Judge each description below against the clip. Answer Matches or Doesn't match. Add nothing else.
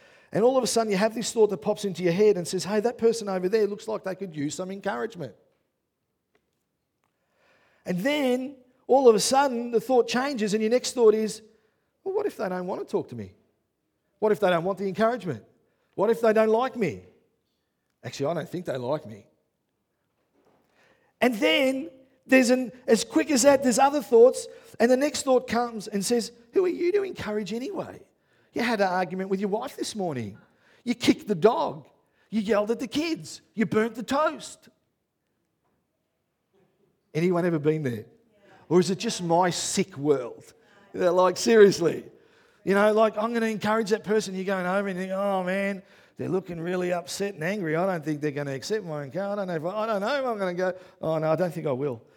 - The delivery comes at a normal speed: Doesn't match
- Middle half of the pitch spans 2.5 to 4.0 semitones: Doesn't match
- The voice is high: Matches